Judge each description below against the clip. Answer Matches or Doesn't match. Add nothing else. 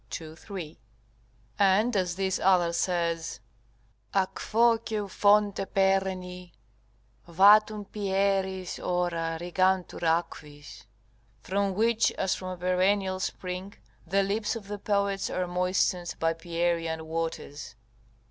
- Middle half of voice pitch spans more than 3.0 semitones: Doesn't match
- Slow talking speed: Matches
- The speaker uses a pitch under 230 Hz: Matches